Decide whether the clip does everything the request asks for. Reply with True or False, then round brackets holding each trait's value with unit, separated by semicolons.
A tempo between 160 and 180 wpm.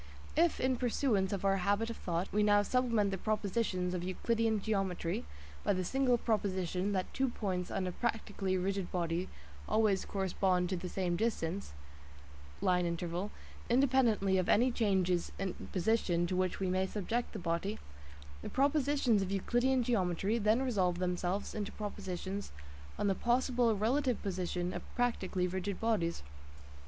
False (150 wpm)